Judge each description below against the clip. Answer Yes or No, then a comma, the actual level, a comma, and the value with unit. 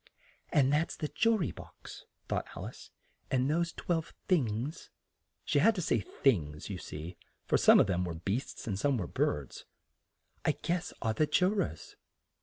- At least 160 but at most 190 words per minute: Yes, average, 175 wpm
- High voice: No, low, 130 Hz